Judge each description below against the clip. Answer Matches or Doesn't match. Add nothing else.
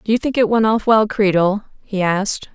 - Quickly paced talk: Matches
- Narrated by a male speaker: Doesn't match